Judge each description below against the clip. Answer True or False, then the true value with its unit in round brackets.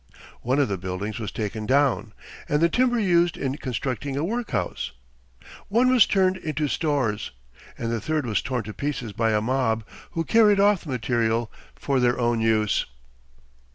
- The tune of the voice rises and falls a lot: True (6.7 semitones)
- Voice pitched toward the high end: False (130 Hz)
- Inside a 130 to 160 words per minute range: False (170 wpm)